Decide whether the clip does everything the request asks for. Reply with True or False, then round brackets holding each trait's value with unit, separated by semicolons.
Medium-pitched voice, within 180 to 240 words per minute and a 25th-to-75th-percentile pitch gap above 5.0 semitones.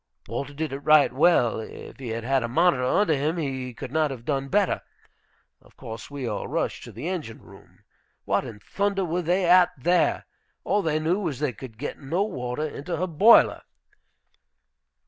True (150 Hz; 185 wpm; 5.5 semitones)